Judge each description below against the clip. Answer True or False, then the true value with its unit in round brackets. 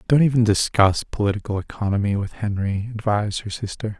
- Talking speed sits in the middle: True (150 wpm)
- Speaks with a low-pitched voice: True (105 Hz)